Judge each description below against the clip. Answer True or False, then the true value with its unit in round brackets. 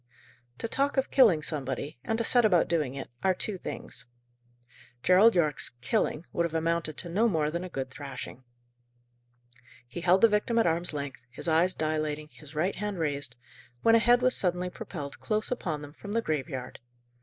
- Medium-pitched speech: True (170 Hz)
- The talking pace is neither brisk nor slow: True (185 wpm)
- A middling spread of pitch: False (5.7 semitones)